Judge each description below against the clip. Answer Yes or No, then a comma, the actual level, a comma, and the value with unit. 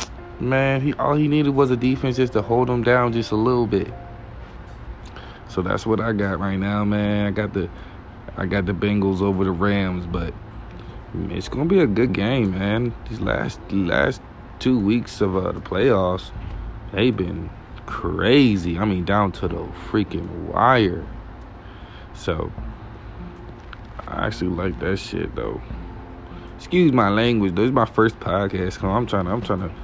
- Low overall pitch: Yes, low, 100 Hz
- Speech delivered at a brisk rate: No, average, 165 wpm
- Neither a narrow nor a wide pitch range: Yes, average, 3.9 semitones